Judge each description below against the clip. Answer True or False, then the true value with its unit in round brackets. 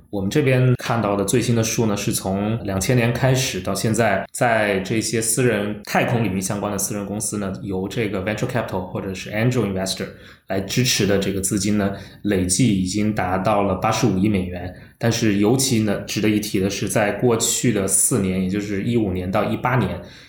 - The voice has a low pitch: True (105 Hz)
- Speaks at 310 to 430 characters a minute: True (360 characters per minute)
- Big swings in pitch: False (3.1 semitones)